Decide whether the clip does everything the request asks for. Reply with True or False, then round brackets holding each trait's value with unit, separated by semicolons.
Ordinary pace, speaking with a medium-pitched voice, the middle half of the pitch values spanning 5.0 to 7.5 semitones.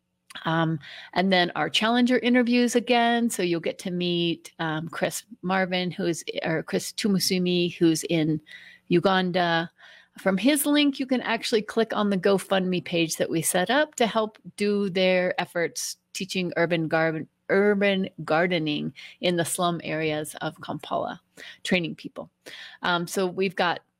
False (150 wpm; 180 Hz; 4.1 semitones)